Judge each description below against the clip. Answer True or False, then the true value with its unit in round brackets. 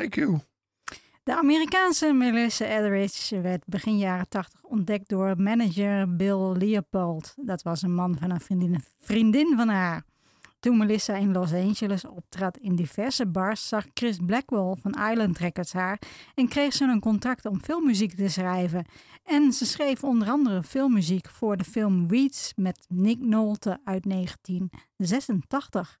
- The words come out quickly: False (150 wpm)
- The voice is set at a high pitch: True (200 Hz)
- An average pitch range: True (4.1 semitones)